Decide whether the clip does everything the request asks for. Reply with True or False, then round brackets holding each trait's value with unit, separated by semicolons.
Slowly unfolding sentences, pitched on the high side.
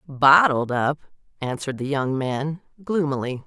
False (120 wpm; 140 Hz)